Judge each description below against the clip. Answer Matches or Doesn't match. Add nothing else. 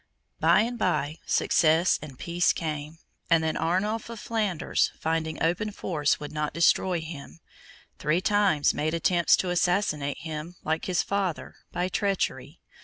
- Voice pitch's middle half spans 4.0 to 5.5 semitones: Doesn't match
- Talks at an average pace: Matches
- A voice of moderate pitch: Matches